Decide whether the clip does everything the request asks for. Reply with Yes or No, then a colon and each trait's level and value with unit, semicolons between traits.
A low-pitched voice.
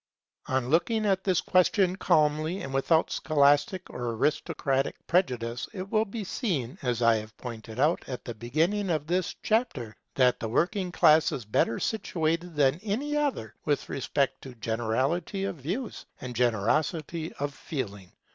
No: medium, 150 Hz